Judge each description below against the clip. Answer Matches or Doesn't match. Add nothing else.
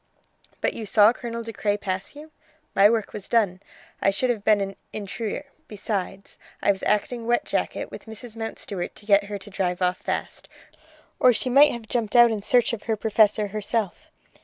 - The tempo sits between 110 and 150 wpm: Doesn't match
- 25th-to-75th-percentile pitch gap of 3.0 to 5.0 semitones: Doesn't match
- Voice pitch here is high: Matches